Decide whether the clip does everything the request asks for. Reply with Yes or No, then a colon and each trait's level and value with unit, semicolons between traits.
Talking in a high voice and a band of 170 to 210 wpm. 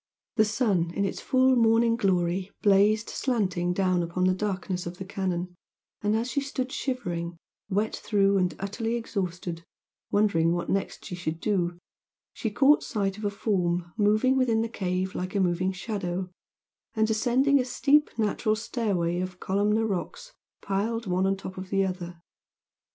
No: high, 195 Hz; average, 160 wpm